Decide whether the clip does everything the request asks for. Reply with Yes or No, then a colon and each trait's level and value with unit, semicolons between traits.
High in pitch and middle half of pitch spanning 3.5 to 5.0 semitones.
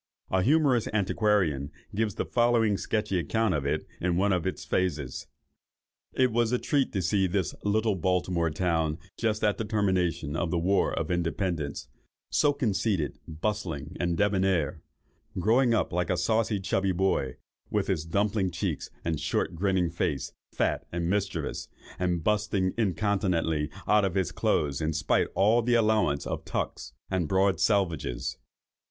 No: very low, 95 Hz; average, 4.1 semitones